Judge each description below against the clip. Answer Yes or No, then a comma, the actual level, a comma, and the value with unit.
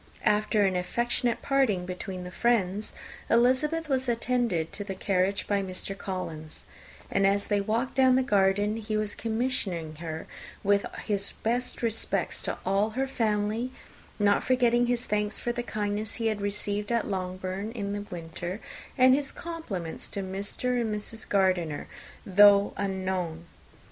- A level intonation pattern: No, average, 3.8 semitones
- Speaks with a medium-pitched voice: No, high, 205 Hz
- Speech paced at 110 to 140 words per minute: No, average, 150 wpm